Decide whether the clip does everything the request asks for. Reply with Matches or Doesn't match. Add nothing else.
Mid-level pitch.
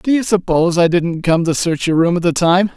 Matches